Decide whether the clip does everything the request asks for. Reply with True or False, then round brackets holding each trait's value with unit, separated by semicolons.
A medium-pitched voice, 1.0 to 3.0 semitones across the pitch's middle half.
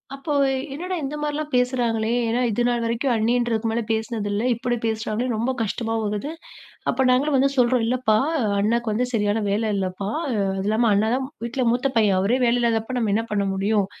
False (235 Hz; 2.5 semitones)